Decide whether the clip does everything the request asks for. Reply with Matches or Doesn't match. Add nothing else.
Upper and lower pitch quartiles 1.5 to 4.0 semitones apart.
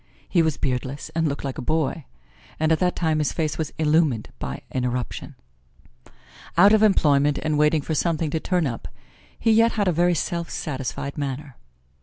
Matches